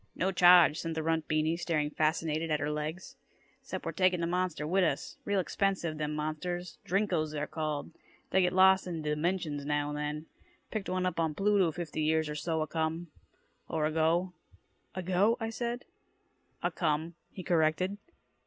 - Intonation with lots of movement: No, average, 3.0 semitones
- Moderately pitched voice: Yes, medium, 165 Hz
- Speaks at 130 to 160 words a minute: No, average, 170 wpm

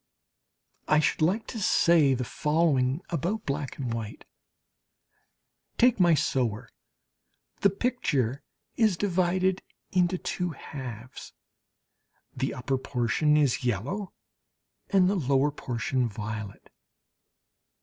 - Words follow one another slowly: Yes, slow, 105 wpm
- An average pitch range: No, wide, 6.3 semitones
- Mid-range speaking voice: Yes, medium, 150 Hz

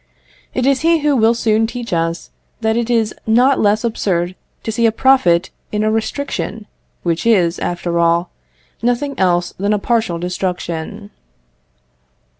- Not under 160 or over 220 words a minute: No, average, 150 wpm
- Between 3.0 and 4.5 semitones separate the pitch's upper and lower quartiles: No, average, 5.1 semitones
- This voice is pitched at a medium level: No, high, 215 Hz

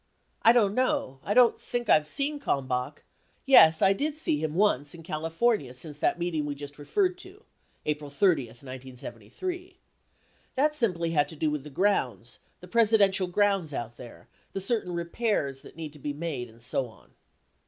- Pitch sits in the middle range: Yes, medium, 165 Hz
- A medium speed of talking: Yes, average, 175 wpm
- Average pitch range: No, wide, 7.1 semitones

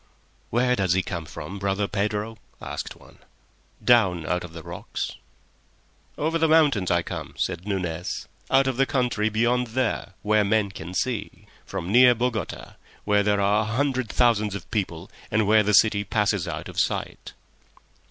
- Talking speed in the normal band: Yes, average, 160 wpm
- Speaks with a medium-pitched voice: No, low, 105 Hz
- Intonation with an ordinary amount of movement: Yes, average, 3.8 semitones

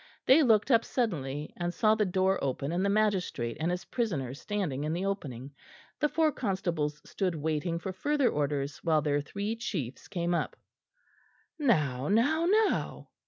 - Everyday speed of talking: Yes, average, 165 wpm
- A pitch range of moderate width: No, wide, 6.7 semitones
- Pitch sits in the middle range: Yes, medium, 180 Hz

